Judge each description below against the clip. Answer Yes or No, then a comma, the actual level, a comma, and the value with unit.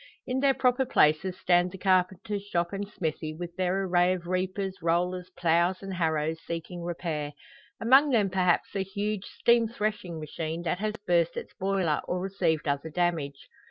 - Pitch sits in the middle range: Yes, medium, 180 Hz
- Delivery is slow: No, average, 165 wpm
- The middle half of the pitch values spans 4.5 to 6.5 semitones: No, average, 2.7 semitones